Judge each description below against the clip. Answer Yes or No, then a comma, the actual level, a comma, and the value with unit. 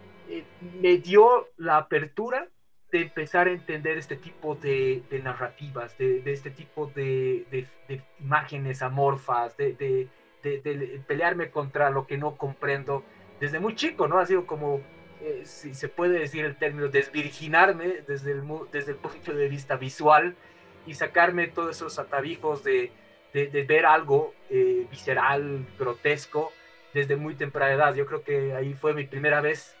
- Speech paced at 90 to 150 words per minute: No, average, 160 wpm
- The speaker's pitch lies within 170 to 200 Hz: No, medium, 150 Hz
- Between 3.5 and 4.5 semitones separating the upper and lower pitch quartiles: Yes, average, 4.1 semitones